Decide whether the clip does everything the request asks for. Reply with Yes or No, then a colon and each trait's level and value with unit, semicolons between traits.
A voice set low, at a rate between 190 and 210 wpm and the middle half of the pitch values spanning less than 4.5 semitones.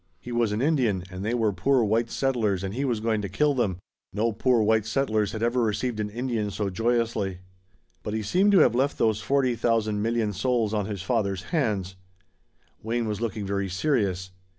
Yes: low, 110 Hz; average, 195 wpm; average, 2.9 semitones